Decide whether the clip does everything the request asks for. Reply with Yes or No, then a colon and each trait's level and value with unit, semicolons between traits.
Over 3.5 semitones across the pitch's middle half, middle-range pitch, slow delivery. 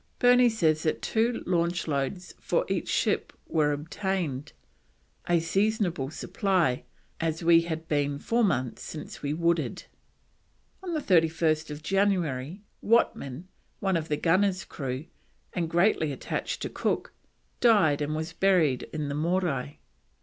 Yes: average, 4.3 semitones; medium, 165 Hz; slow, 130 wpm